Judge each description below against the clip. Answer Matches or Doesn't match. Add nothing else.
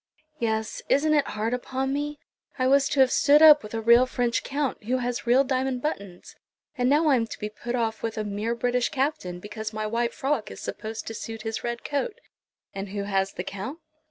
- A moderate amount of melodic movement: Matches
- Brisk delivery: Matches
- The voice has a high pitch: Matches